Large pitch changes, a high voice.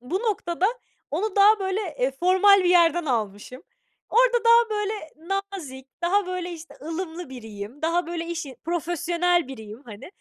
Yes: wide, 5.9 semitones; very high, 345 Hz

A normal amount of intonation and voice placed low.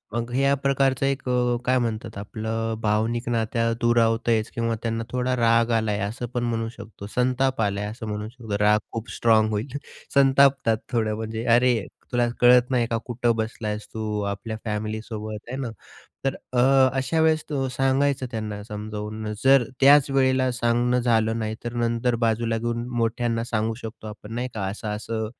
No: narrow, 2.2 semitones; low, 115 Hz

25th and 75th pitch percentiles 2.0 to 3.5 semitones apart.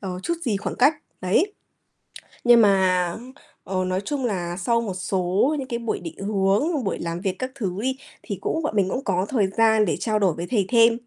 No: average, 4.5 semitones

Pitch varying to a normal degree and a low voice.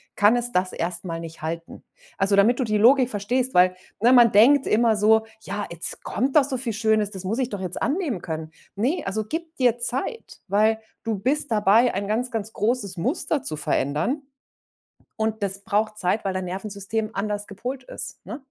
No: average, 4.0 semitones; high, 215 Hz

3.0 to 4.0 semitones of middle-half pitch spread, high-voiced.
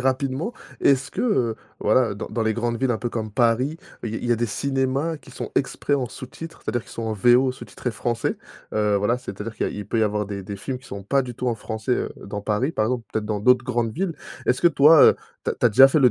No: average, 3.4 semitones; low, 120 Hz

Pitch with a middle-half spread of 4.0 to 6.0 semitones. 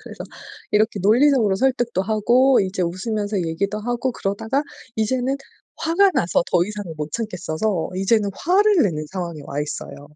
Yes: average, 5.2 semitones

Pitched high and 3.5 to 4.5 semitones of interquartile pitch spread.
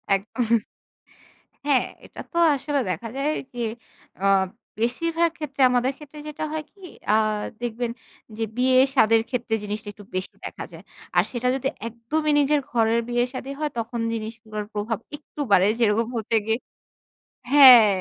Yes: high, 240 Hz; average, 3.8 semitones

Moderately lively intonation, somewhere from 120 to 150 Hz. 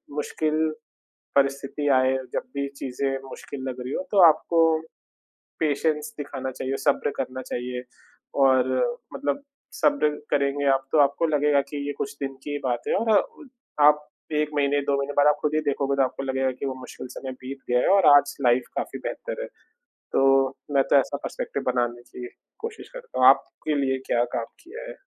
No: narrow, 2.1 semitones; medium, 140 Hz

